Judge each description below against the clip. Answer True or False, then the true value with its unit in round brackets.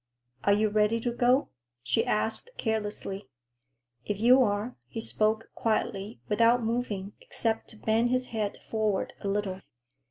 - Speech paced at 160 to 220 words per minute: False (140 wpm)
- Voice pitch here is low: False (220 Hz)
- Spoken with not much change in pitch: True (2.2 semitones)